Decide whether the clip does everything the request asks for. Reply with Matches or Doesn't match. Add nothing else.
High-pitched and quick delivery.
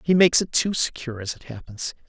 Doesn't match